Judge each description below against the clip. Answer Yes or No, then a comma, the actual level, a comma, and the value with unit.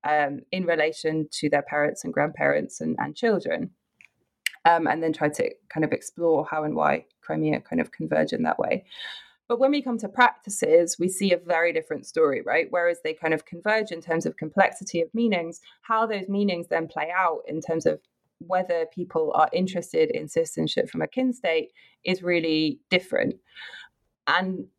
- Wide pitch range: Yes, wide, 6.0 semitones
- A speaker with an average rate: Yes, average, 185 wpm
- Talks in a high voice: No, medium, 175 Hz